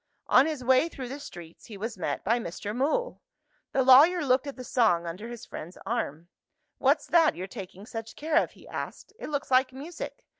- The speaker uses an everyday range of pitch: No, wide, 5.7 semitones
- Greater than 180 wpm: Yes, average, 200 wpm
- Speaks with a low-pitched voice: No, very high, 250 Hz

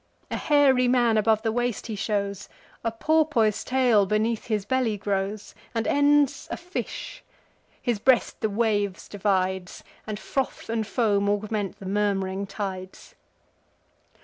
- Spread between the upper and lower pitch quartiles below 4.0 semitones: Yes, average, 3.3 semitones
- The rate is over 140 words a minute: No, slow, 135 wpm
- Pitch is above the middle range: Yes, high, 215 Hz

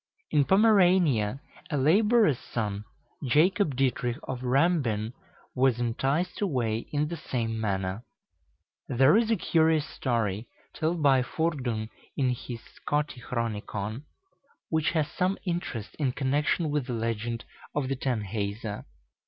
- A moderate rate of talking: No, slow, 120 wpm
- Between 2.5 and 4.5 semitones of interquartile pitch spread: No, wide, 5.5 semitones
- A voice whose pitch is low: Yes, low, 130 Hz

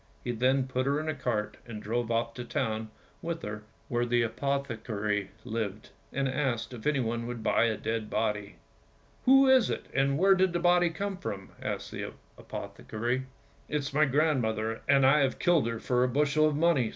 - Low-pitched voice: Yes, low, 125 Hz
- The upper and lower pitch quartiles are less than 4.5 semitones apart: No, average, 4.9 semitones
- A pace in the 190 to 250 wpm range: Yes, average, 200 wpm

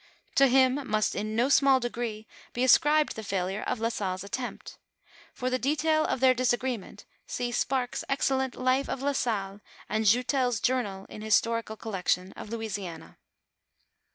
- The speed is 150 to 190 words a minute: Yes, average, 155 wpm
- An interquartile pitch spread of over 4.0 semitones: No, average, 3.5 semitones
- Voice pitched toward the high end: Yes, high, 240 Hz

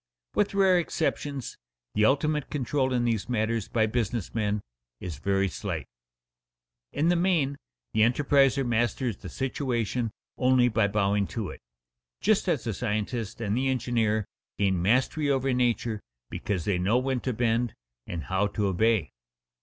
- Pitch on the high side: No, low, 120 Hz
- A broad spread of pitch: No, average, 4.0 semitones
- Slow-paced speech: No, average, 150 wpm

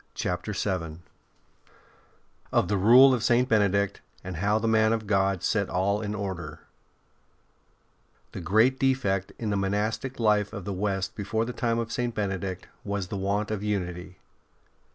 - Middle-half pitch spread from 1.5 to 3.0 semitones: Yes, narrow, 2.4 semitones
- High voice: No, low, 100 Hz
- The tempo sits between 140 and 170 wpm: Yes, average, 155 wpm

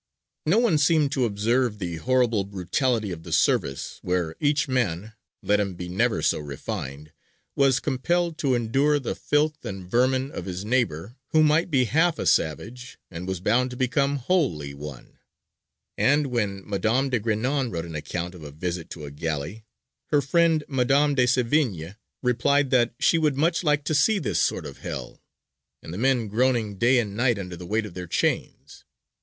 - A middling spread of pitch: No, wide, 7.3 semitones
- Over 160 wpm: Yes, average, 180 wpm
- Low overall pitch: Yes, low, 120 Hz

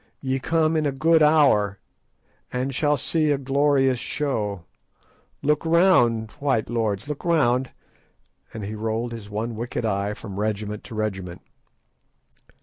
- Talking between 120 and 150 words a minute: Yes, average, 140 wpm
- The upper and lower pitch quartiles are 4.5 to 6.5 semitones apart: Yes, wide, 5.4 semitones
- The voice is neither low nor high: No, low, 120 Hz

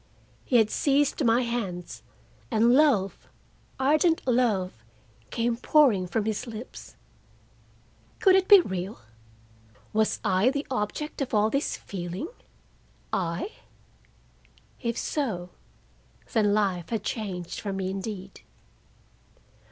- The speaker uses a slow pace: Yes, slow, 110 wpm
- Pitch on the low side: No, high, 220 Hz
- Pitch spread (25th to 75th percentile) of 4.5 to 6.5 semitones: Yes, average, 5.2 semitones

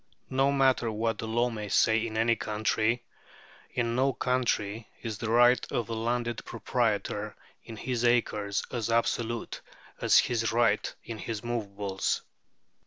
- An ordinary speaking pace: Yes, average, 145 wpm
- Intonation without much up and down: Yes, narrow, 1.8 semitones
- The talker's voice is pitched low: Yes, low, 115 Hz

